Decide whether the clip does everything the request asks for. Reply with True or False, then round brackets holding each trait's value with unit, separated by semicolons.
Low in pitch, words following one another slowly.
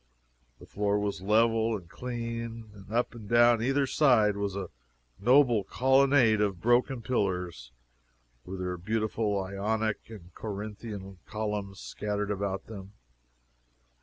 True (105 Hz; 125 wpm)